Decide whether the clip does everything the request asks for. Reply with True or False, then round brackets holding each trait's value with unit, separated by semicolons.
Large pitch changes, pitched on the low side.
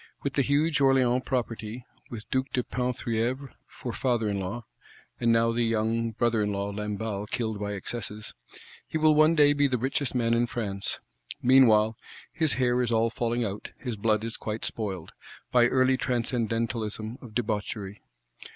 False (3.0 semitones; 115 Hz)